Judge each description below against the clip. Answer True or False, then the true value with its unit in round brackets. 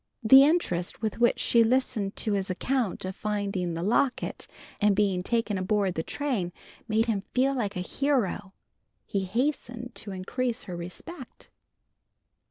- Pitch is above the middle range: True (210 Hz)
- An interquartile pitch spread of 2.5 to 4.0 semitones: False (4.7 semitones)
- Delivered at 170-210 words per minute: False (150 wpm)